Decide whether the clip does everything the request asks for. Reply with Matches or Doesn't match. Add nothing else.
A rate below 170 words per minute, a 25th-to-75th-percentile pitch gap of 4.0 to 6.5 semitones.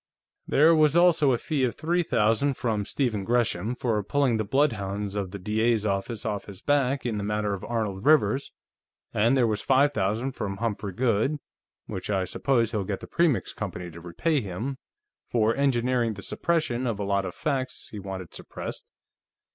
Doesn't match